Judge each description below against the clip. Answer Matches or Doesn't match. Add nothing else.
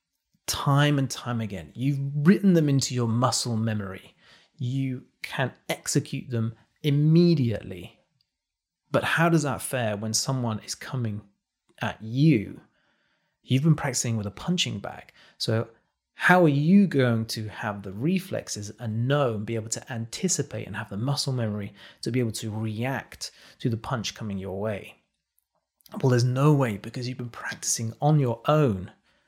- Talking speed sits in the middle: Matches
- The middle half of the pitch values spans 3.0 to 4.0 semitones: Doesn't match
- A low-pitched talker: Matches